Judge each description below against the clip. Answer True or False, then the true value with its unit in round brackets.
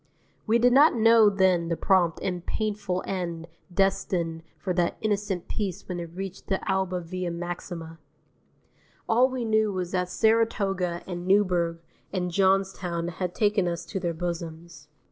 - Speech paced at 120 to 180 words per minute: True (150 wpm)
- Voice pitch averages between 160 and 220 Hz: True (185 Hz)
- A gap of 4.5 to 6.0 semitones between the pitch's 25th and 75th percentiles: False (2.8 semitones)